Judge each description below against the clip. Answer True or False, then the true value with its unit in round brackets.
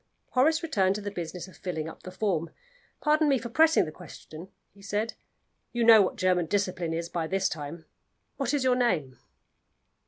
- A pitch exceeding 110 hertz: True (190 Hz)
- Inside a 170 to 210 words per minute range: True (185 wpm)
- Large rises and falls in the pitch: True (5.9 semitones)